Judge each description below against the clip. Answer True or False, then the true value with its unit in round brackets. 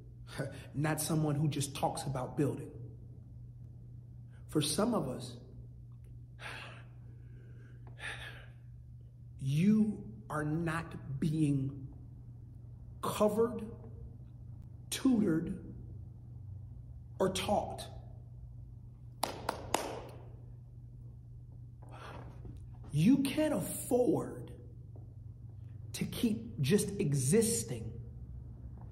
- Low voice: True (120 Hz)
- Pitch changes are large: False (3.7 semitones)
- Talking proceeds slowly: True (55 wpm)